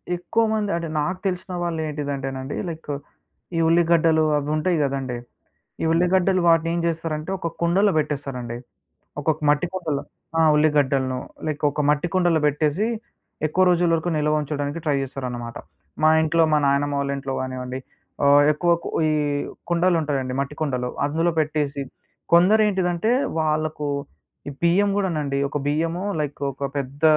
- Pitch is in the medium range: Yes, medium, 155 Hz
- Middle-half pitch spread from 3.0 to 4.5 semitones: Yes, average, 3.3 semitones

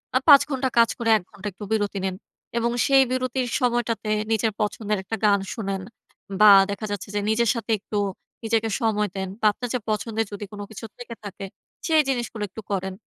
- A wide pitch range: No, narrow, 2.5 semitones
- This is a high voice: Yes, high, 220 Hz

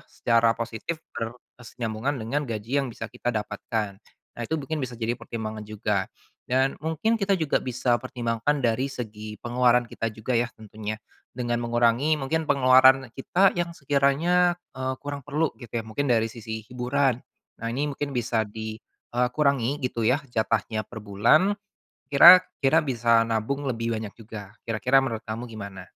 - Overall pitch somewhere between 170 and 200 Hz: No, low, 120 Hz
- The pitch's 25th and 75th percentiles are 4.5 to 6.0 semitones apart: No, average, 3.8 semitones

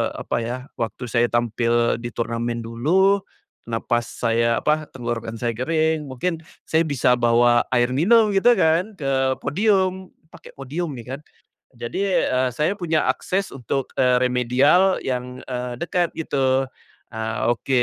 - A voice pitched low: Yes, low, 130 Hz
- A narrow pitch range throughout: No, wide, 5.5 semitones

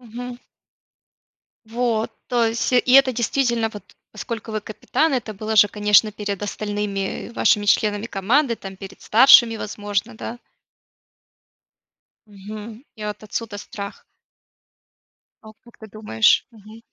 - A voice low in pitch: No, high, 215 Hz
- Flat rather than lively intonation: Yes, narrow, 2.3 semitones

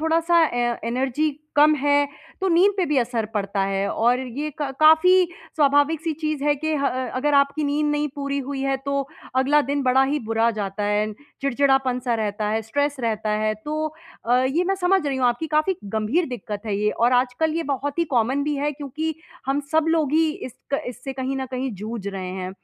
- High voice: Yes, very high, 275 Hz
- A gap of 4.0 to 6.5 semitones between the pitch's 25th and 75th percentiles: Yes, average, 4.4 semitones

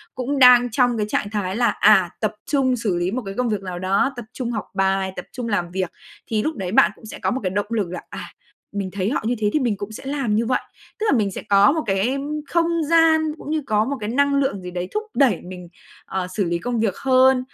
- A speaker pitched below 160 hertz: No, high, 220 Hz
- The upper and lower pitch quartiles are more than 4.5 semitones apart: Yes, average, 5.1 semitones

